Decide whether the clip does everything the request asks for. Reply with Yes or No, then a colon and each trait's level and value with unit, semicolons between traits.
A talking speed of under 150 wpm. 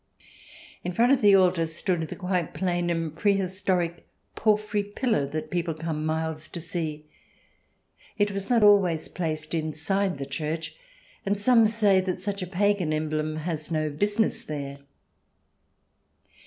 Yes: average, 140 wpm